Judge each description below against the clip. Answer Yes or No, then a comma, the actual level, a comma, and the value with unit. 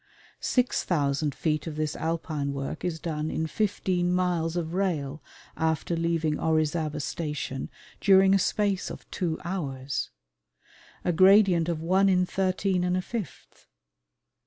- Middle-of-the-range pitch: Yes, medium, 165 Hz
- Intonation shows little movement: No, average, 3.2 semitones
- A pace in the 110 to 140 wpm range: Yes, slow, 135 wpm